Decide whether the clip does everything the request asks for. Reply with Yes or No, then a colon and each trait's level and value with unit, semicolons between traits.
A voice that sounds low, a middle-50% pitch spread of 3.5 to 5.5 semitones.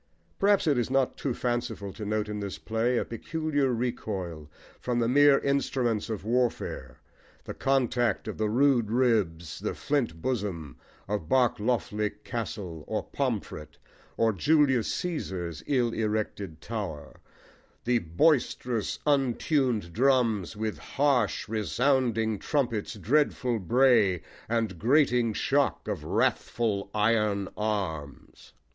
Yes: low, 115 Hz; average, 3.9 semitones